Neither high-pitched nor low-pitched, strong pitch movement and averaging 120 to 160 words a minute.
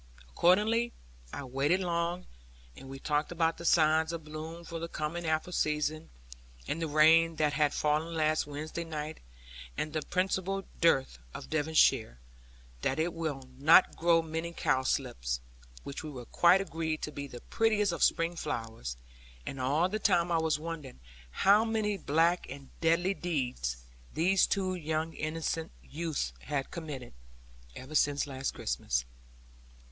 No: medium, 160 Hz; average, 2.9 semitones; average, 145 wpm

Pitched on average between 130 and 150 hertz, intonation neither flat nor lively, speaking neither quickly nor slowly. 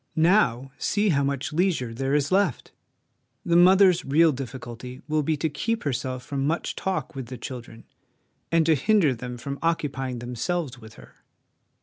Yes: medium, 140 Hz; average, 4.8 semitones; average, 160 wpm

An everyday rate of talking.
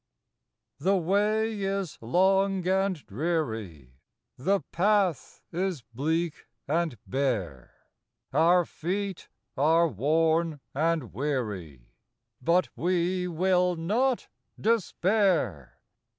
No: slow, 85 wpm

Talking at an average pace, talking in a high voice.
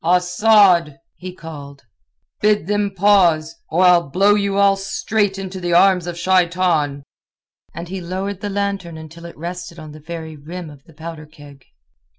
No: average, 160 wpm; medium, 175 Hz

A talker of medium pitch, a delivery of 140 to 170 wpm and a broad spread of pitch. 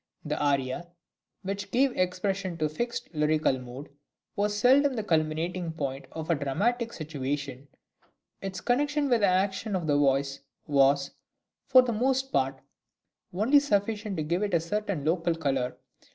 Yes: medium, 175 Hz; average, 165 wpm; wide, 6.4 semitones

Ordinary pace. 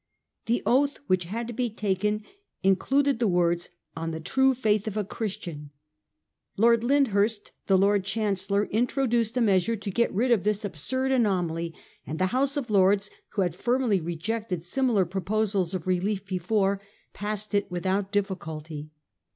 Yes: average, 160 wpm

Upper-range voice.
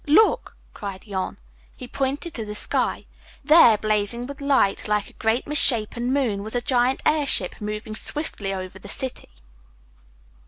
Yes: high, 230 Hz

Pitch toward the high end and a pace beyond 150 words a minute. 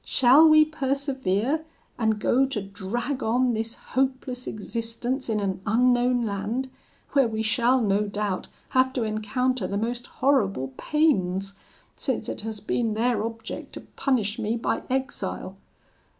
No: high, 235 Hz; average, 140 wpm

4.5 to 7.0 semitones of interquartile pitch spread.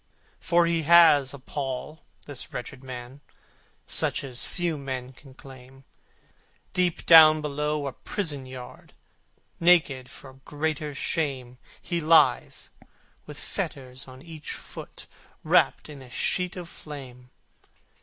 No: average, 3.5 semitones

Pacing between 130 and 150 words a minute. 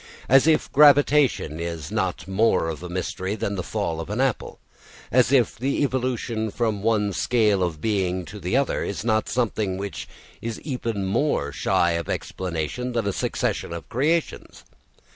No: average, 165 wpm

